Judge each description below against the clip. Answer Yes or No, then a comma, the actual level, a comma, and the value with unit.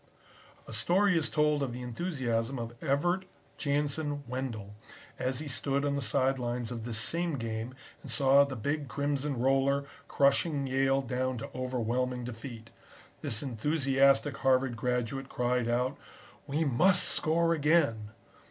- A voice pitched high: No, low, 135 Hz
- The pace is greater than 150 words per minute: No, average, 145 wpm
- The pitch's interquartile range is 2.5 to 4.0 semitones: Yes, average, 2.9 semitones